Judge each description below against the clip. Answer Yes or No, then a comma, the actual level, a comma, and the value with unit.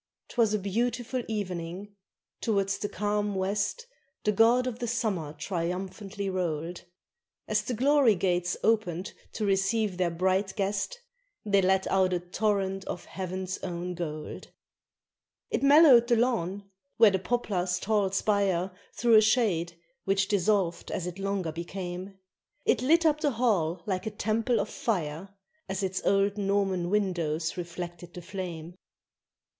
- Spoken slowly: No, average, 145 wpm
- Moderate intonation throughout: Yes, average, 3.2 semitones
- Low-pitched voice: No, high, 195 Hz